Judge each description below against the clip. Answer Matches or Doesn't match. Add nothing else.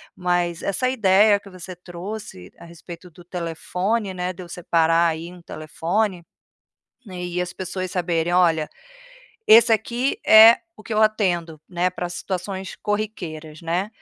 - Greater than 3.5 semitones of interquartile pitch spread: Doesn't match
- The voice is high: Doesn't match